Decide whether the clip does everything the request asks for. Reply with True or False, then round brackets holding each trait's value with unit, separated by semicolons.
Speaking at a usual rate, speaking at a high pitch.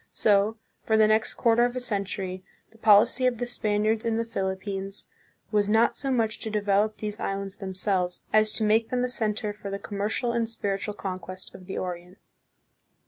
True (190 wpm; 210 Hz)